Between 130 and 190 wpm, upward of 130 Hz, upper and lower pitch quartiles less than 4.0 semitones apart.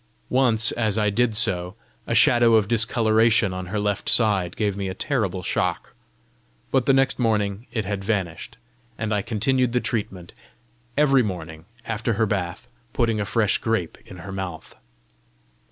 No: average, 160 wpm; low, 105 Hz; average, 3.3 semitones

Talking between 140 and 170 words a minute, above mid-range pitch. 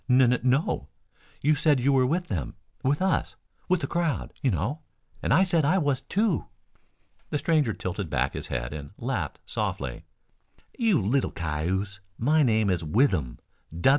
No: average, 165 wpm; low, 125 Hz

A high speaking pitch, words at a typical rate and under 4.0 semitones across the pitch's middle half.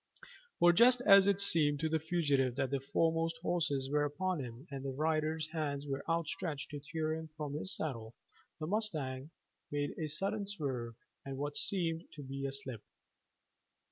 No: medium, 155 Hz; average, 175 wpm; average, 3.2 semitones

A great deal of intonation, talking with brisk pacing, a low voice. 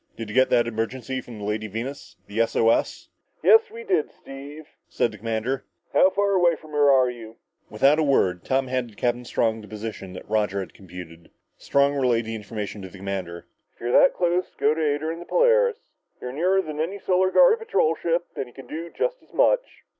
Yes: wide, 7.5 semitones; fast, 215 wpm; low, 130 Hz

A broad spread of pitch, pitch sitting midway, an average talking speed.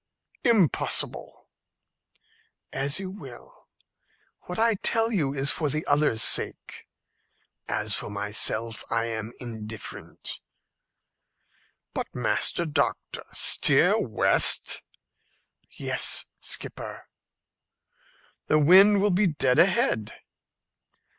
No: wide, 8.7 semitones; medium, 145 Hz; slow, 90 wpm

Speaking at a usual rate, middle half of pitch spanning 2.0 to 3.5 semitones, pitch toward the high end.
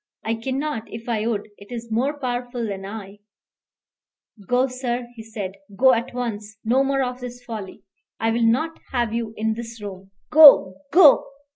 Yes: average, 175 wpm; narrow, 2.5 semitones; high, 235 Hz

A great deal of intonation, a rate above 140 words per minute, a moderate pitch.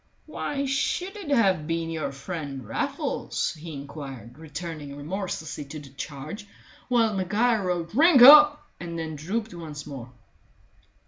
No: wide, 7.4 semitones; slow, 135 wpm; medium, 165 Hz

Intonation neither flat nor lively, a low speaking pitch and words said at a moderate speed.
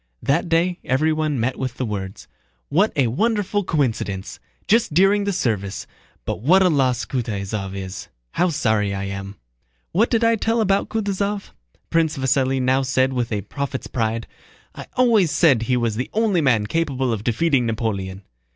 No: wide, 8.0 semitones; low, 130 Hz; average, 165 wpm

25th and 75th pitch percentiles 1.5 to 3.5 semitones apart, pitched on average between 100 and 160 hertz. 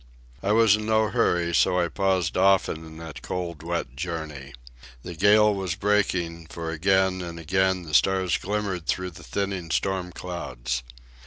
No: average, 2.8 semitones; very low, 90 Hz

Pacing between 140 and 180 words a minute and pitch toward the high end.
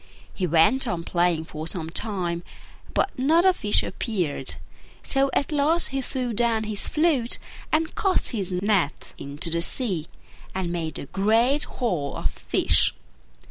Yes: average, 150 wpm; high, 205 Hz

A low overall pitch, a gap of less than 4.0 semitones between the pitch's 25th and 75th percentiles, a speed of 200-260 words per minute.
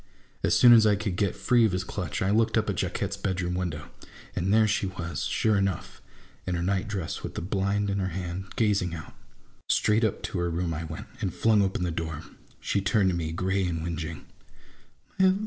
Yes: very low, 95 Hz; average, 2.9 semitones; fast, 205 wpm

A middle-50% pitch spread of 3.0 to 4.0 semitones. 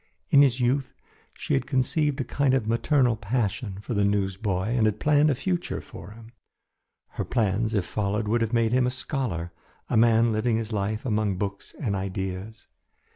Yes: average, 3.7 semitones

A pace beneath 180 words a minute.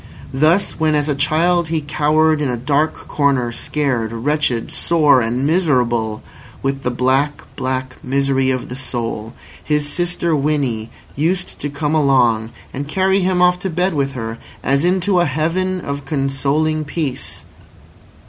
Yes: average, 150 wpm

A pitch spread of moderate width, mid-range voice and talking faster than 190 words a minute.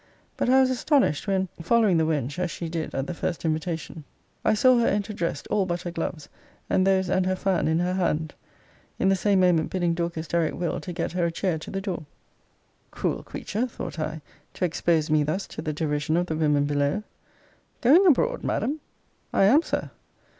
Yes: average, 3.4 semitones; medium, 175 Hz; fast, 205 wpm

